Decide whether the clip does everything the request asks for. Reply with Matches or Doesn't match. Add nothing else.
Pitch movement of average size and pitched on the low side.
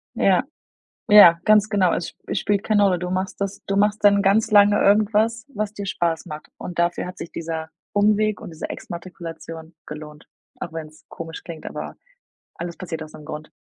Doesn't match